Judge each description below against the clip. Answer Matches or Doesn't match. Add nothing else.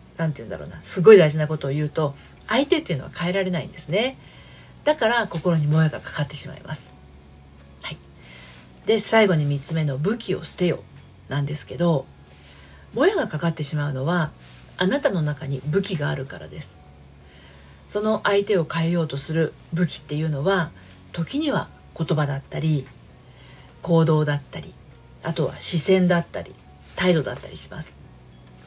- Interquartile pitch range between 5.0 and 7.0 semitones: Matches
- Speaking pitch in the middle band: Matches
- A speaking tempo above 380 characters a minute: Doesn't match